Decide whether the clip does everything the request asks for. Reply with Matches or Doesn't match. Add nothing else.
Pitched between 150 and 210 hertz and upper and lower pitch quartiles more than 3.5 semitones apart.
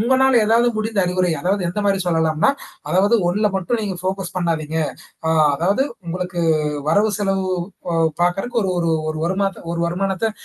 Doesn't match